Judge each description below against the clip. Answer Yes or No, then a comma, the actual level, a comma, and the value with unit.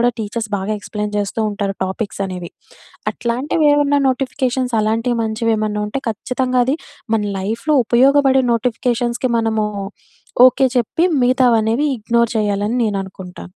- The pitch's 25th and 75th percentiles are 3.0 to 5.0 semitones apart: Yes, average, 3.3 semitones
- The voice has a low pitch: No, high, 230 Hz